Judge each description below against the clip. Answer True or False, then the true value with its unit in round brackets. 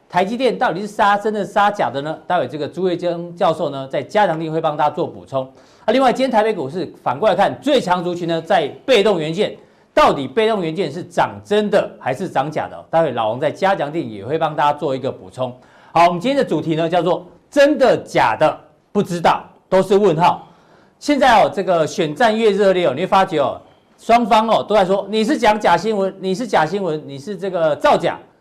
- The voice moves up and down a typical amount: True (4.7 semitones)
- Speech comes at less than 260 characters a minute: False (320 characters per minute)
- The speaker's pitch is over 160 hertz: True (185 Hz)